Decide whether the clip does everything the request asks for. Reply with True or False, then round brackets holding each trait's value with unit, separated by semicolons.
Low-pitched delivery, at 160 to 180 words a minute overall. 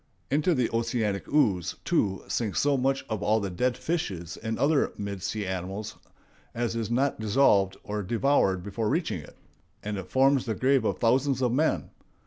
True (115 Hz; 170 wpm)